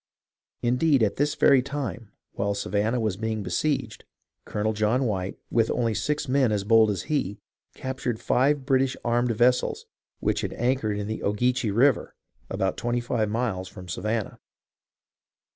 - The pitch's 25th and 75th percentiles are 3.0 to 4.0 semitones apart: Yes, average, 3.6 semitones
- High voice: No, low, 115 Hz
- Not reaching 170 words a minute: Yes, average, 150 wpm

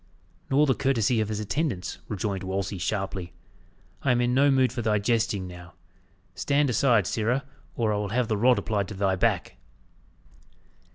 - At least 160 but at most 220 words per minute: Yes, average, 170 wpm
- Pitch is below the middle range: Yes, low, 110 Hz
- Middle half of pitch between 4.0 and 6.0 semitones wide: Yes, average, 4.3 semitones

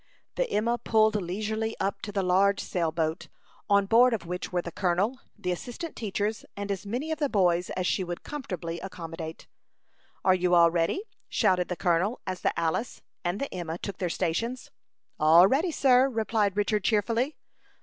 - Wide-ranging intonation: No, average, 4.3 semitones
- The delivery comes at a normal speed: Yes, average, 180 wpm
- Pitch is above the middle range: Yes, high, 195 Hz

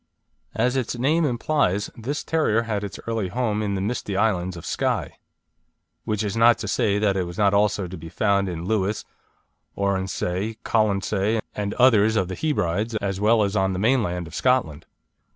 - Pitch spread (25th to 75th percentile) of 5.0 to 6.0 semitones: No, average, 3.1 semitones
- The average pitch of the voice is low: Yes, low, 105 Hz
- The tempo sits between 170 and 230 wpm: Yes, average, 180 wpm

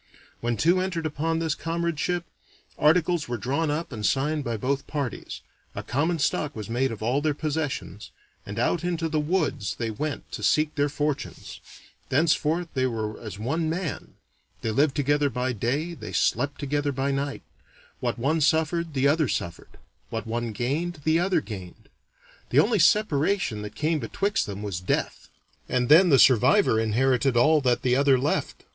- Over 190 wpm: No, average, 170 wpm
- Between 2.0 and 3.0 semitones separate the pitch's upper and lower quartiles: No, average, 4.9 semitones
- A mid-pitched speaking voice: Yes, medium, 145 Hz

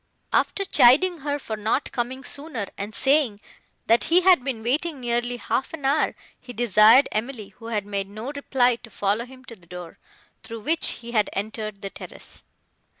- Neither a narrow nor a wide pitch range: Yes, average, 4.3 semitones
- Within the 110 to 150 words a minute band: No, average, 175 wpm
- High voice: Yes, high, 240 Hz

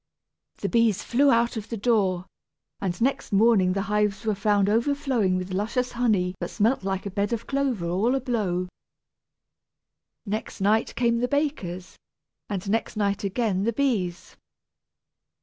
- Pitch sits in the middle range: No, high, 210 Hz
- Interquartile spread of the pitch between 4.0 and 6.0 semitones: No, average, 3.6 semitones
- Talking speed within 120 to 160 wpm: Yes, average, 150 wpm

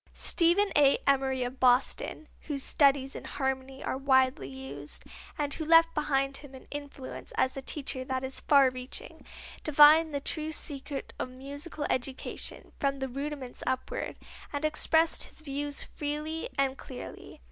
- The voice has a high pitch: Yes, very high, 275 Hz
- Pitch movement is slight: Yes, narrow, 2.2 semitones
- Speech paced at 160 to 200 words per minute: No, average, 150 wpm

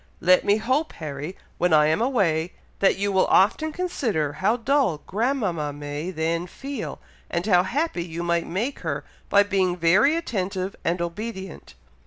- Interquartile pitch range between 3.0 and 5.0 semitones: No, wide, 5.4 semitones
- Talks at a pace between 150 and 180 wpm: Yes, average, 160 wpm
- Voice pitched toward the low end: No, medium, 185 Hz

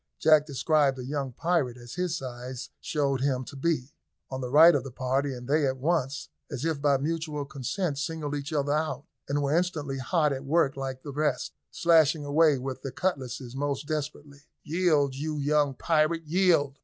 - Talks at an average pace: Yes, average, 185 wpm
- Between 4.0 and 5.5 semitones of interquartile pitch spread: No, narrow, 2.6 semitones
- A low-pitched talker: No, medium, 145 Hz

